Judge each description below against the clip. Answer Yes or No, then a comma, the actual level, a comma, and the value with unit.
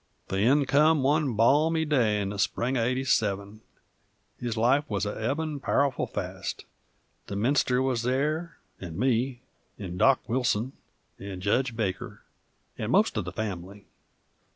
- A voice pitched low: Yes, low, 120 Hz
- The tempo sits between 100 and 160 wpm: Yes, average, 145 wpm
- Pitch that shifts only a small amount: No, average, 4.9 semitones